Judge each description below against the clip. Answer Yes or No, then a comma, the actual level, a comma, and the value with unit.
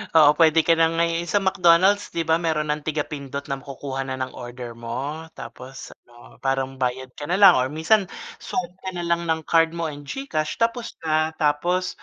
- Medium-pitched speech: Yes, medium, 155 Hz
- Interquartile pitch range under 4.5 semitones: Yes, average, 3.9 semitones